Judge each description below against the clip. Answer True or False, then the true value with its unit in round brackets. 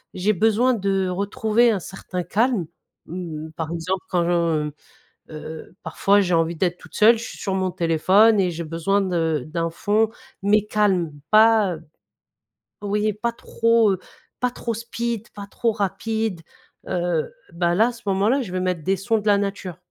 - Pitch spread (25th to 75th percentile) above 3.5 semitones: True (4.0 semitones)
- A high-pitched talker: True (195 Hz)